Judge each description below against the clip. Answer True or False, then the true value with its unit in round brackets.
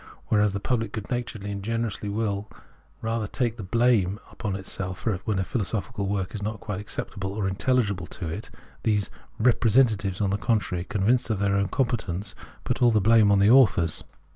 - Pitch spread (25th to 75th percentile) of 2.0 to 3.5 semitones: True (2.7 semitones)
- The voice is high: False (105 Hz)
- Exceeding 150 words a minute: True (190 wpm)